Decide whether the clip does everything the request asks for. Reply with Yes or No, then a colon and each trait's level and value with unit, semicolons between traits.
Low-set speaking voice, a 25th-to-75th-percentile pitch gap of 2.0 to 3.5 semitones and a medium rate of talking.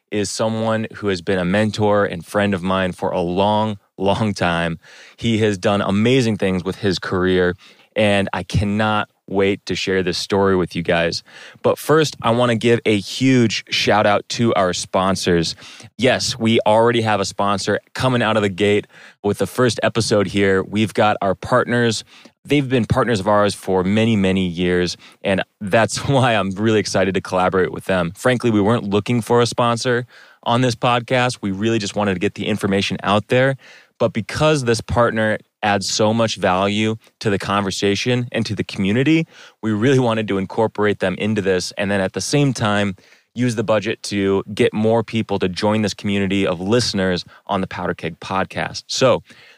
Yes: low, 105 Hz; average, 3.0 semitones; average, 185 wpm